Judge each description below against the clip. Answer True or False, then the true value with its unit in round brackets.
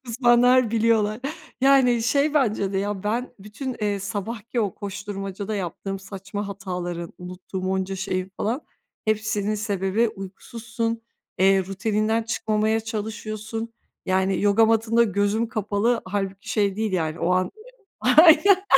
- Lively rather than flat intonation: False (2.8 semitones)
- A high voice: True (210 Hz)